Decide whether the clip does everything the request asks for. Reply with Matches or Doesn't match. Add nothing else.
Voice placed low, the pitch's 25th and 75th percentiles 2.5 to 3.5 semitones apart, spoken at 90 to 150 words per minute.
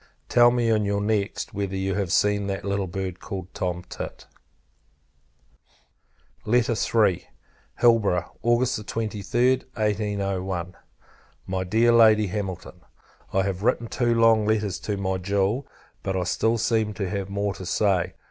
Matches